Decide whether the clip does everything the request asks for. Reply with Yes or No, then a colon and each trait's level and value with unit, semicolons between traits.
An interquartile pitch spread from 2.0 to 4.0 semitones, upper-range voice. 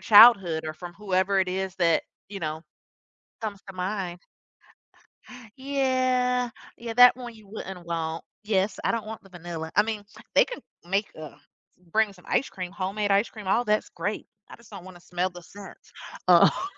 Yes: average, 3.7 semitones; high, 195 Hz